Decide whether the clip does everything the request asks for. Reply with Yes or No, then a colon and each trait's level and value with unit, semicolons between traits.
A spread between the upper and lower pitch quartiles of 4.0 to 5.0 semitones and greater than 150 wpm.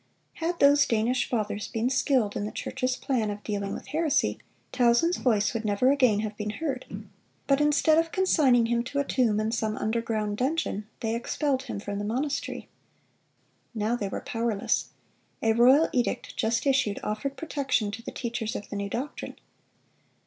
Yes: average, 4.4 semitones; average, 170 wpm